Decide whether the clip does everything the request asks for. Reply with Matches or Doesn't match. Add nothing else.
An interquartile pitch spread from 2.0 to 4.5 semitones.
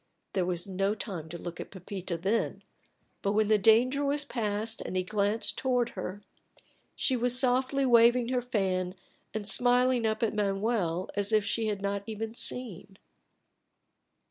Matches